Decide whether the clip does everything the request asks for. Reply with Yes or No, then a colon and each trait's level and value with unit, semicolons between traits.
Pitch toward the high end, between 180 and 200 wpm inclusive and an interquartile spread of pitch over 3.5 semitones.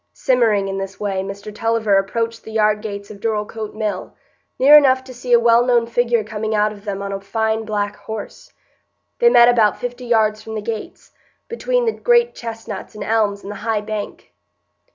No: high, 220 Hz; average, 190 wpm; narrow, 2.4 semitones